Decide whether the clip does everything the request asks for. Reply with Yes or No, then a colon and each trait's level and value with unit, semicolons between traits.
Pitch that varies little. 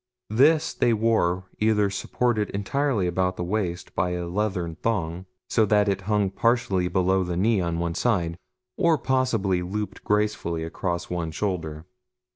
No: average, 3.7 semitones